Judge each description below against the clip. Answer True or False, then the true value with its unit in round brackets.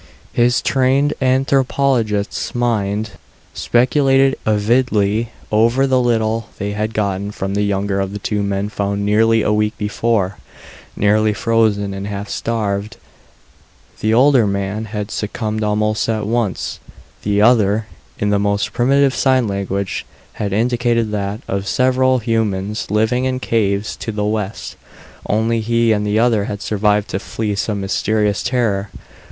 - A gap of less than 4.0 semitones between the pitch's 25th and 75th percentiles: True (2.5 semitones)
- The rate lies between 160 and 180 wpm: False (140 wpm)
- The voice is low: True (110 Hz)